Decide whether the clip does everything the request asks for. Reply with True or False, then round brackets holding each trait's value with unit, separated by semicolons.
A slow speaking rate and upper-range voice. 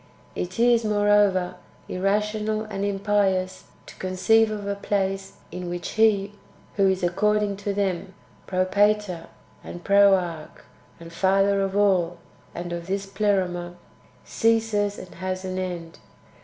True (130 wpm; 195 Hz)